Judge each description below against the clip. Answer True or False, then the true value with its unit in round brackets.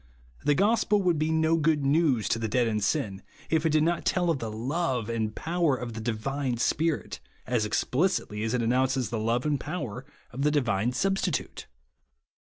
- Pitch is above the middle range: False (135 Hz)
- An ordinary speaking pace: True (190 wpm)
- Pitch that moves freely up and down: True (5.8 semitones)